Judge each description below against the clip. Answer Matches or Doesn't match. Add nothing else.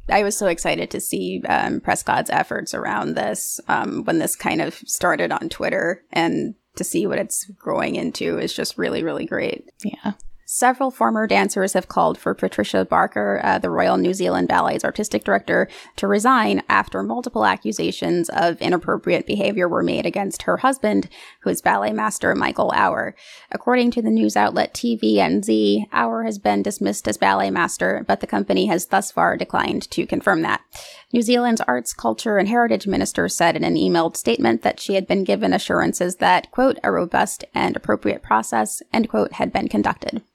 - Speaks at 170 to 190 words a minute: Matches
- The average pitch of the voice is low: Doesn't match